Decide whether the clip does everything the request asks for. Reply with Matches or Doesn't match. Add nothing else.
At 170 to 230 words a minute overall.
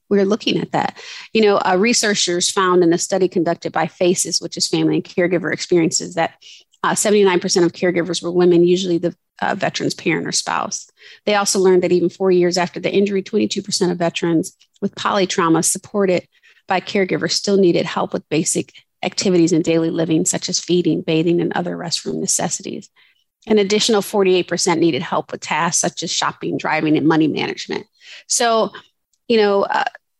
Matches